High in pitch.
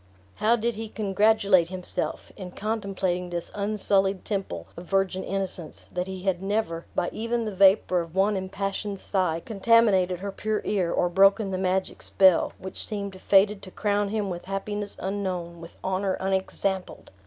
Yes: high, 195 Hz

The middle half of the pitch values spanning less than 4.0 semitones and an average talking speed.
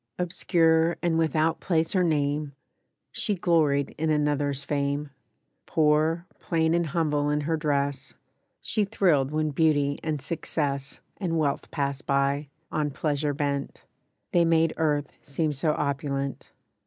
No: narrow, 2.4 semitones; slow, 130 wpm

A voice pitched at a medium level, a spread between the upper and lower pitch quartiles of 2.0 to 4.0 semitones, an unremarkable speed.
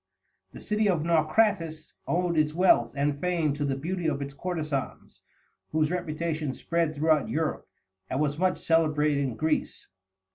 Yes: medium, 155 Hz; narrow, 2.6 semitones; average, 150 wpm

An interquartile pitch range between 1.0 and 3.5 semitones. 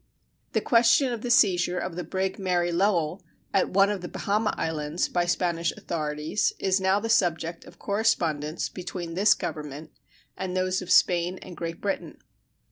Yes: average, 2.8 semitones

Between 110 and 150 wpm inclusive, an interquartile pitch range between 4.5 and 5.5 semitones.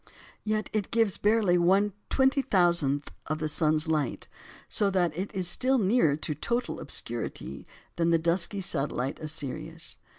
Yes: average, 140 wpm; average, 5.0 semitones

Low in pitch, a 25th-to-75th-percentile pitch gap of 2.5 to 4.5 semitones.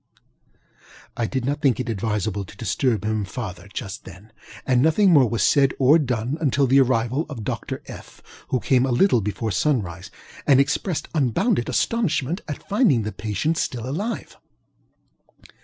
No: low, 125 Hz; average, 5.1 semitones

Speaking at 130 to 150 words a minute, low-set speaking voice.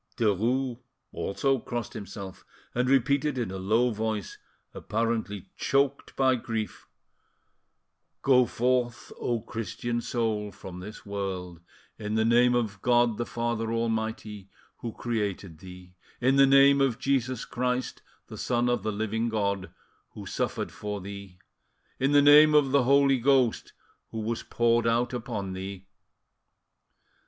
Yes: slow, 135 wpm; low, 115 Hz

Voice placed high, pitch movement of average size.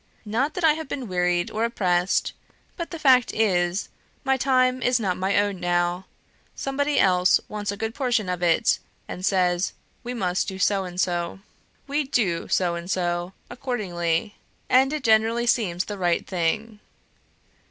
No: high, 200 Hz; wide, 5.7 semitones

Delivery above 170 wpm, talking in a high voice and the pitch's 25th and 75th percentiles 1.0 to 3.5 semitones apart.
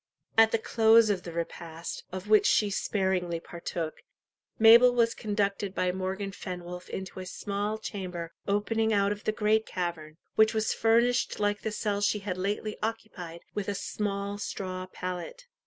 No: average, 160 wpm; high, 200 Hz; average, 3.0 semitones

